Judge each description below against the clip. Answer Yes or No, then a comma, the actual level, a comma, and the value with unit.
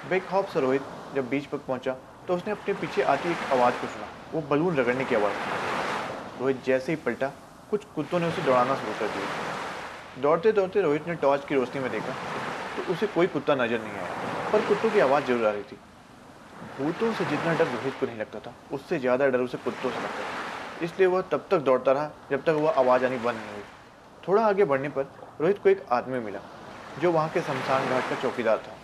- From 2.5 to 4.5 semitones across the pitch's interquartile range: No, wide, 5.5 semitones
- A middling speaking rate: No, fast, 225 wpm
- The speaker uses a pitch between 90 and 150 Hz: Yes, medium, 140 Hz